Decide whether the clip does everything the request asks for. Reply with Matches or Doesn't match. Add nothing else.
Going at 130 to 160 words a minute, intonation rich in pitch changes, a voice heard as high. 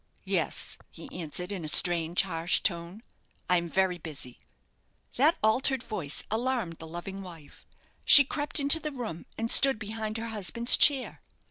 Matches